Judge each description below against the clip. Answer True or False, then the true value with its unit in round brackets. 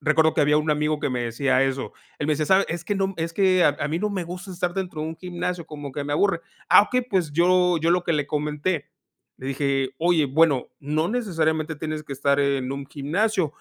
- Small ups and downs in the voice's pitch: False (3.7 semitones)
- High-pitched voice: False (155 Hz)